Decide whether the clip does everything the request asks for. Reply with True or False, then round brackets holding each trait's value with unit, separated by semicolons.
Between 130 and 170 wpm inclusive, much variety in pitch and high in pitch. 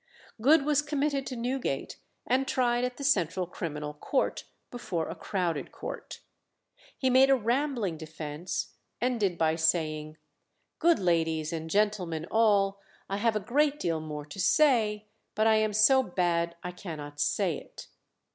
True (150 wpm; 7.5 semitones; 200 Hz)